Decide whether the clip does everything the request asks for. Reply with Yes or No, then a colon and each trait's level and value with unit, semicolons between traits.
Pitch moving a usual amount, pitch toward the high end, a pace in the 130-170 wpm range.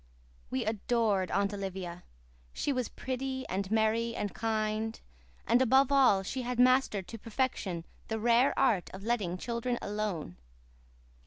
Yes: average, 3.9 semitones; high, 220 Hz; average, 140 wpm